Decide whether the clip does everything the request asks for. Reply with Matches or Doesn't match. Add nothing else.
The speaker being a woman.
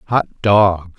Doesn't match